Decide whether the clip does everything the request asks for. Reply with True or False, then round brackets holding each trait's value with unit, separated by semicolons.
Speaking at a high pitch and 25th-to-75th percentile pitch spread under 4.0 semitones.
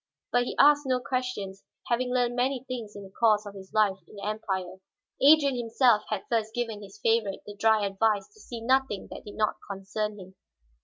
True (220 Hz; 3.5 semitones)